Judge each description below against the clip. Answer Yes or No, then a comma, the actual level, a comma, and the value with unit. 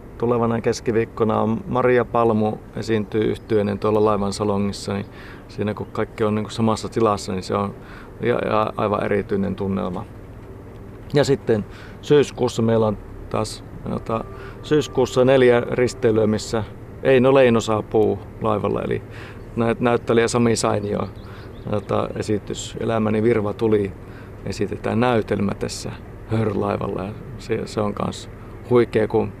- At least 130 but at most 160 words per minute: No, average, 120 wpm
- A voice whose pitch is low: Yes, low, 110 Hz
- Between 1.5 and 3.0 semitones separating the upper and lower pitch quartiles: Yes, narrow, 2.4 semitones